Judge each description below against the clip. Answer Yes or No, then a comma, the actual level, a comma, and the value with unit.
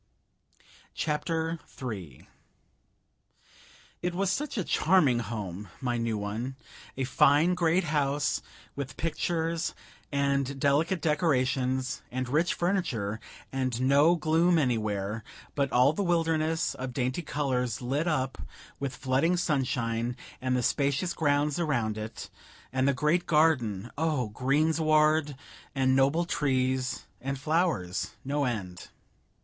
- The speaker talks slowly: Yes, slow, 120 wpm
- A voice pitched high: No, medium, 140 Hz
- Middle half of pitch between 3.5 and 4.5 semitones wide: Yes, average, 4.2 semitones